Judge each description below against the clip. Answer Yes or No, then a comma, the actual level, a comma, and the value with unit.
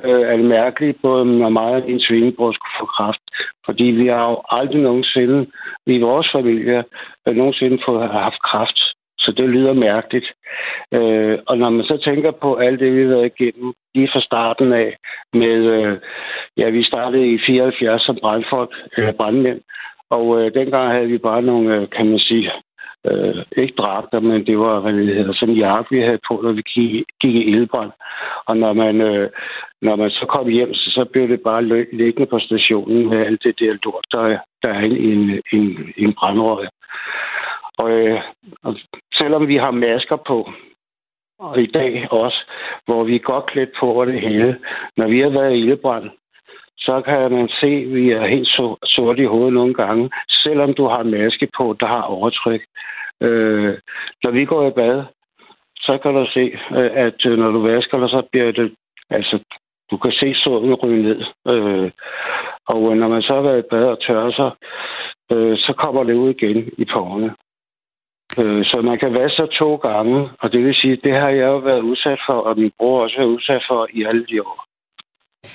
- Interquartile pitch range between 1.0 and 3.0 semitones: Yes, average, 2.7 semitones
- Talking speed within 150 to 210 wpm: Yes, average, 195 wpm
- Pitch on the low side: Yes, low, 120 Hz